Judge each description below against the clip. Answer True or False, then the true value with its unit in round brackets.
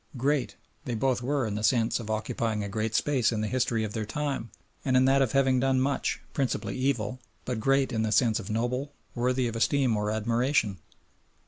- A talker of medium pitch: False (120 Hz)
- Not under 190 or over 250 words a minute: True (205 wpm)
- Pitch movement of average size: True (3.3 semitones)